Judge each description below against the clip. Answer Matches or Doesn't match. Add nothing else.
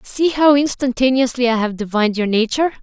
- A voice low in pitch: Doesn't match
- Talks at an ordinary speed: Matches